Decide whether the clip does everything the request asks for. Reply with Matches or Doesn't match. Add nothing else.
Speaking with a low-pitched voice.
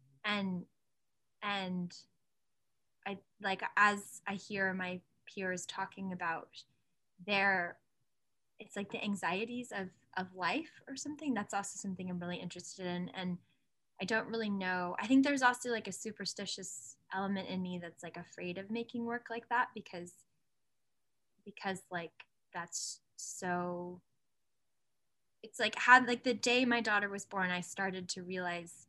Doesn't match